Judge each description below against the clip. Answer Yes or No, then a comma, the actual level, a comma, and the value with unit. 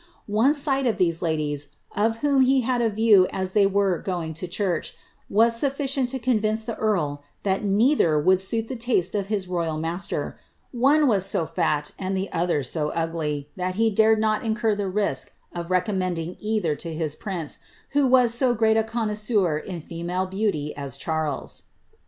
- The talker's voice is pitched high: Yes, high, 195 Hz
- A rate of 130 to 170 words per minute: No, average, 180 wpm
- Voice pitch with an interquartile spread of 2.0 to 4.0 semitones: No, average, 5.0 semitones